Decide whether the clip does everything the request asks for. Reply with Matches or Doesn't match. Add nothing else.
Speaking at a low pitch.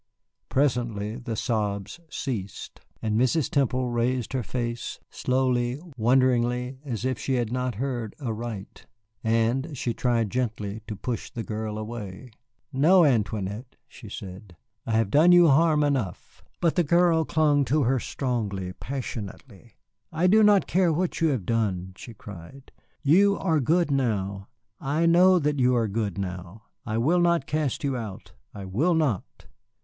Matches